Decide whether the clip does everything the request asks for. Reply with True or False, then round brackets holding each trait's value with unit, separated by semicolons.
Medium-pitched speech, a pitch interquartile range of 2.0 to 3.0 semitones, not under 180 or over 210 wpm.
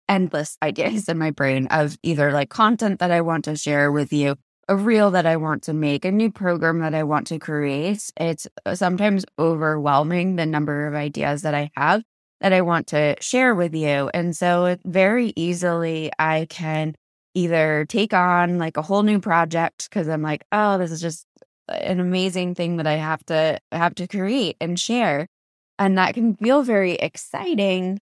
False (170 Hz; 3.8 semitones; 190 wpm)